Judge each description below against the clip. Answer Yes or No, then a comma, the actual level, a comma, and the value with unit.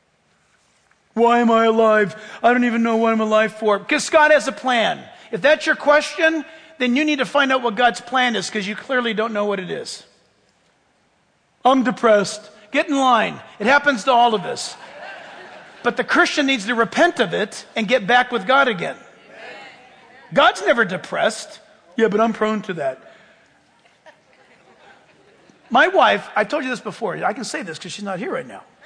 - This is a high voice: Yes, high, 240 Hz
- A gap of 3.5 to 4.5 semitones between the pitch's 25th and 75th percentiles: Yes, average, 4.2 semitones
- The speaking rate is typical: Yes, average, 185 wpm